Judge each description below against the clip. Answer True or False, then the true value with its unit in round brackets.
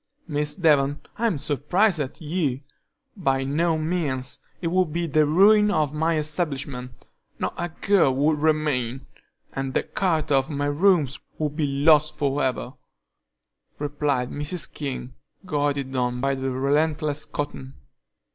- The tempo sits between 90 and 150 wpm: True (135 wpm)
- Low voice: False (150 Hz)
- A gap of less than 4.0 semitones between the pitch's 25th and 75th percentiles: True (2.8 semitones)